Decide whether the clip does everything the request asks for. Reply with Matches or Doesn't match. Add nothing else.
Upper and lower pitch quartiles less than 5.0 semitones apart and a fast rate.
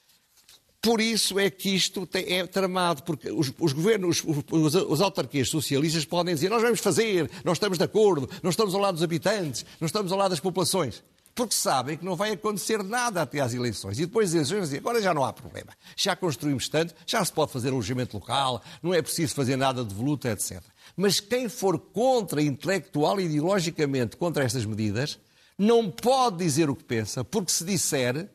Doesn't match